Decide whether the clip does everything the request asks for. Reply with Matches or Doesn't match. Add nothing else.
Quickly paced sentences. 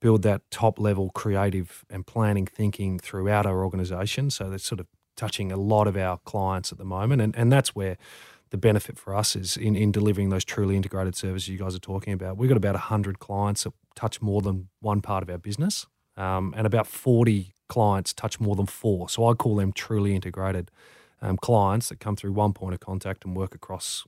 Matches